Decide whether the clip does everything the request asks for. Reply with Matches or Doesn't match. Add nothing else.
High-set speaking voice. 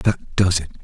Doesn't match